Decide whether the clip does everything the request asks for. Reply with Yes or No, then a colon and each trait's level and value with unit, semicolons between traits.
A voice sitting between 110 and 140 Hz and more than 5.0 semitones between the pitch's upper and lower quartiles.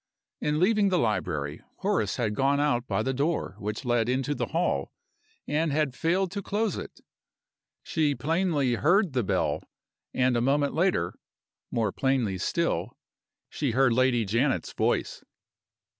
Yes: low, 135 Hz; wide, 5.5 semitones